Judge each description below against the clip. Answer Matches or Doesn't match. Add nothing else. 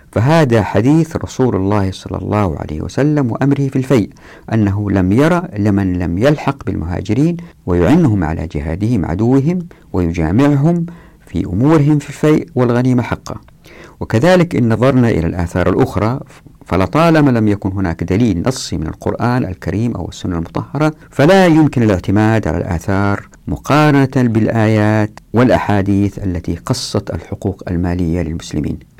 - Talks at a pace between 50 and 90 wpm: Doesn't match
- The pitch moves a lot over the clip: Matches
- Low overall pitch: Matches